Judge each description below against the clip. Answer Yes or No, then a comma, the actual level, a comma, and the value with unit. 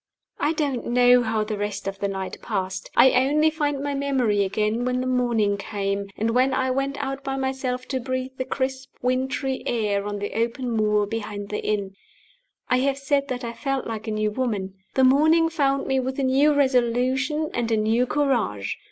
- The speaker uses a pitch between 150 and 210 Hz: No, very high, 250 Hz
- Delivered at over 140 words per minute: Yes, average, 195 wpm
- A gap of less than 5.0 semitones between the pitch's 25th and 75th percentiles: Yes, average, 4.1 semitones